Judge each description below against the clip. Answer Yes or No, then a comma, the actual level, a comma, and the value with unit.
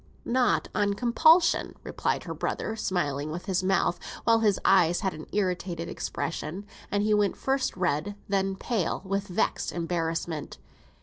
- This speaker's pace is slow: No, average, 145 wpm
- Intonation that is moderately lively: Yes, average, 3.3 semitones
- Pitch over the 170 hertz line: Yes, high, 190 Hz